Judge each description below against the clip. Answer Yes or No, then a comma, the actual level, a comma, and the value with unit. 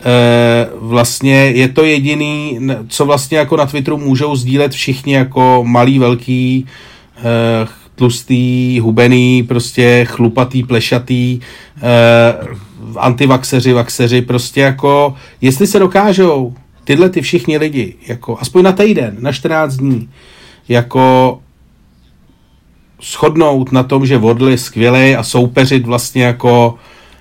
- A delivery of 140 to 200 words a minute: No, slow, 115 wpm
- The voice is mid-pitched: No, low, 125 Hz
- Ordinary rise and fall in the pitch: No, narrow, 2.3 semitones